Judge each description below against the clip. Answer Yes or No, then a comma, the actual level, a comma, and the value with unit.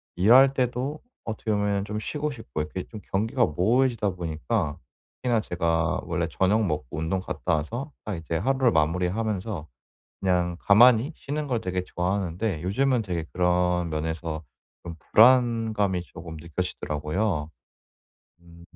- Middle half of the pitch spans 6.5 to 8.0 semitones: No, average, 5.1 semitones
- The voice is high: No, very low, 95 Hz